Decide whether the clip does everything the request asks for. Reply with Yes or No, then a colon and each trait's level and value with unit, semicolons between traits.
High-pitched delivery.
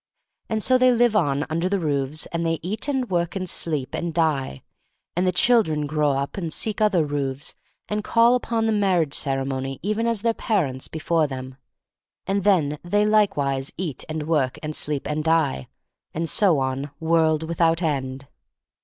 No: medium, 165 Hz